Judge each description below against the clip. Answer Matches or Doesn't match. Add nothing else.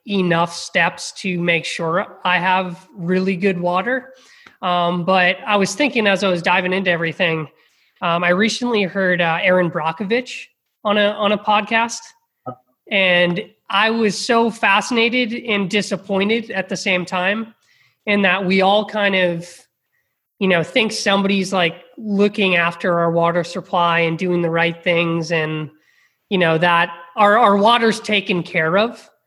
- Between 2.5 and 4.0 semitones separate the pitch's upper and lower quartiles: Matches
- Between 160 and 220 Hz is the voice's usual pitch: Matches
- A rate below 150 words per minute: Doesn't match